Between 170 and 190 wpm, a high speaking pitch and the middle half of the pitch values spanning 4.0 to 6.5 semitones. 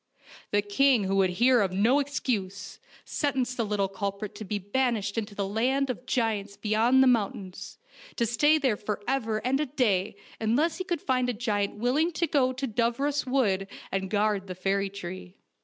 Yes: average, 185 wpm; high, 220 Hz; average, 4.6 semitones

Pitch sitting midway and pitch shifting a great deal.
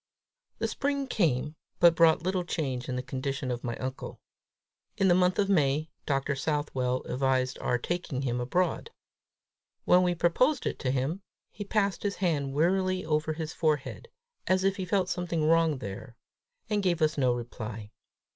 Yes: medium, 155 Hz; wide, 5.7 semitones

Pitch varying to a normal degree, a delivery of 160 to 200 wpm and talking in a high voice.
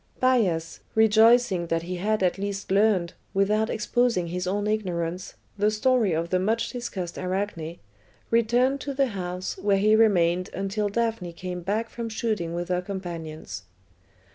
No: average, 3.8 semitones; average, 150 wpm; high, 195 Hz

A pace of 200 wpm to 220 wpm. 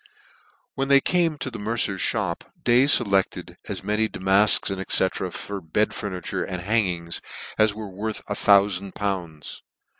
No: average, 145 wpm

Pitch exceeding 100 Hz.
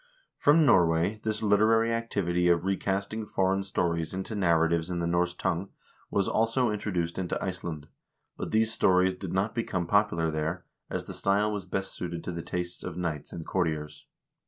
No: very low, 95 Hz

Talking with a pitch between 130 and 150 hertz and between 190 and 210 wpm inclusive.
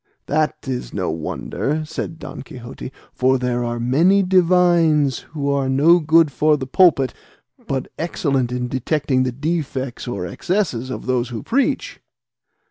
No: medium, 140 Hz; average, 145 wpm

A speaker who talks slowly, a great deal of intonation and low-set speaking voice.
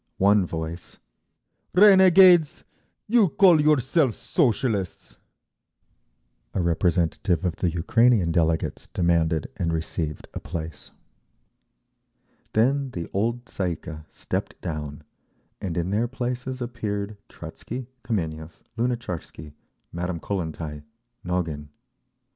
Yes: slow, 100 wpm; wide, 7.0 semitones; very low, 95 Hz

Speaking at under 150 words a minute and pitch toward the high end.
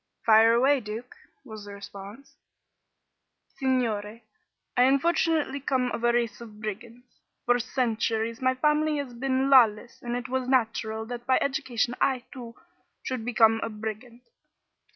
Yes: average, 140 wpm; high, 240 Hz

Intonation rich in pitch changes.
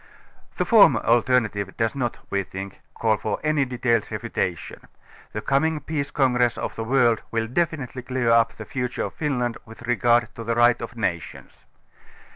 No: narrow, 2.5 semitones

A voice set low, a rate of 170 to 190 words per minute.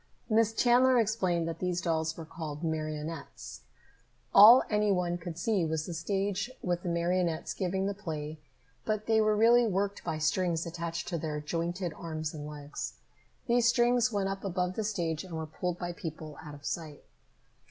No: medium, 175 Hz; average, 175 wpm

